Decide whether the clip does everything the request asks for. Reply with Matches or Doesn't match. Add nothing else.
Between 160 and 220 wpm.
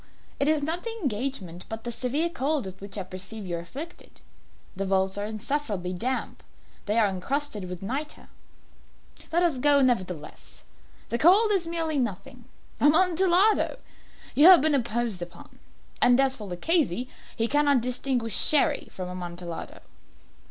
Doesn't match